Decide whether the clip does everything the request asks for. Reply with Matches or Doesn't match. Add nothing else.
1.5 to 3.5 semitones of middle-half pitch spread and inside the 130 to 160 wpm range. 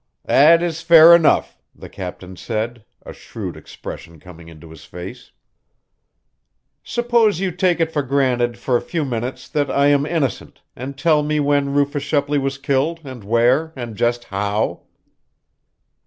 Doesn't match